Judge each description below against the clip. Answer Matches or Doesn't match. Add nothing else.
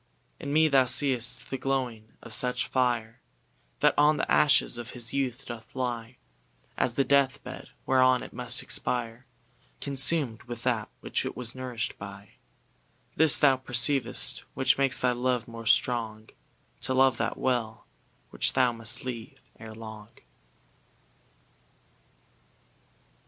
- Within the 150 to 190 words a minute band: Doesn't match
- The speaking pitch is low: Matches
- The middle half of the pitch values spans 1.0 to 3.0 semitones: Matches